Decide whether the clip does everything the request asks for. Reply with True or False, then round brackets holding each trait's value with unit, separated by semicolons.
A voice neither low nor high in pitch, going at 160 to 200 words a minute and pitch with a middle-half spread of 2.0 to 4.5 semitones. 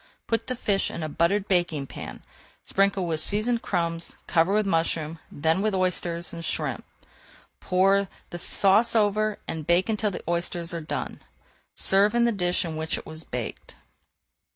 True (180 Hz; 165 wpm; 3.5 semitones)